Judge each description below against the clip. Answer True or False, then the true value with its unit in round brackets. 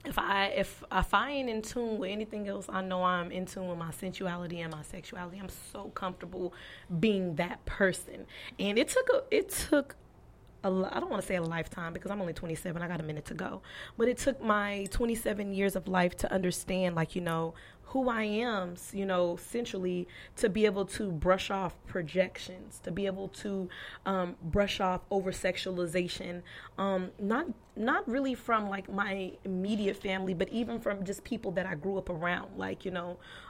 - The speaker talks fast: False (195 wpm)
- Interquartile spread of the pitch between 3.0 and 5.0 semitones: False (2.5 semitones)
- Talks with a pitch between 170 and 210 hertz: True (190 Hz)